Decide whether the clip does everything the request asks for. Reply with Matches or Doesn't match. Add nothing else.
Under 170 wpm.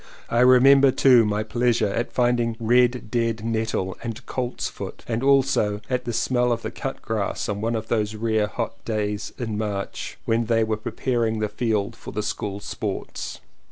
Doesn't match